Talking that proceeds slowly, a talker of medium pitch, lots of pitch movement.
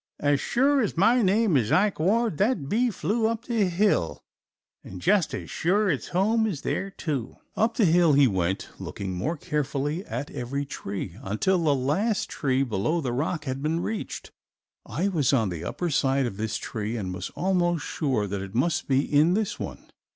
No: average, 190 wpm; medium, 155 Hz; wide, 7.6 semitones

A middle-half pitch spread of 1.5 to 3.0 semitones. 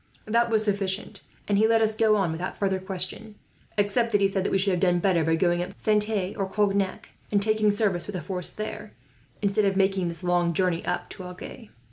Yes: narrow, 2.6 semitones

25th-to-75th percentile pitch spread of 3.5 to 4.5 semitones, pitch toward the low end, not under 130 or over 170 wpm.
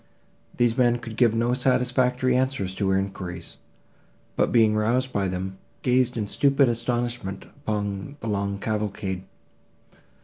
Yes: average, 4.0 semitones; low, 115 Hz; slow, 135 wpm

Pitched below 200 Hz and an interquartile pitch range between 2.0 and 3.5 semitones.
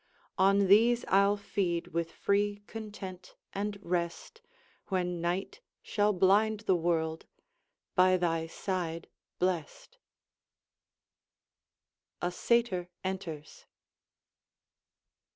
Yes: medium, 185 Hz; average, 2.9 semitones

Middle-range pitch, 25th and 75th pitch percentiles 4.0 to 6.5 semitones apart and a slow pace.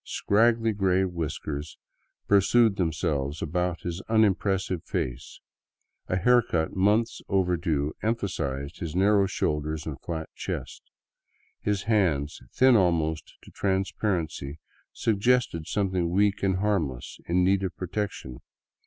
No: very low, 90 Hz; average, 4.3 semitones; slow, 115 wpm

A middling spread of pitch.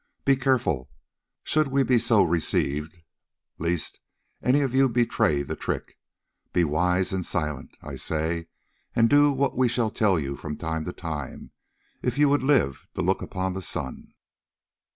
No: wide, 8.4 semitones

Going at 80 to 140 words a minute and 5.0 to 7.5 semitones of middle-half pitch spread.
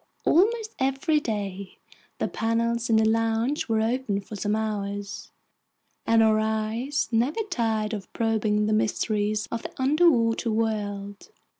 No: slow, 135 wpm; narrow, 2.0 semitones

